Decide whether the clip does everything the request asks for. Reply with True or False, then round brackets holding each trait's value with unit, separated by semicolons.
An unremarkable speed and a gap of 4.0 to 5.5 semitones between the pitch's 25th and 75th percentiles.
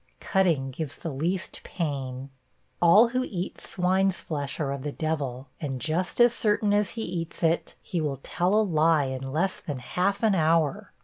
True (180 wpm; 5.2 semitones)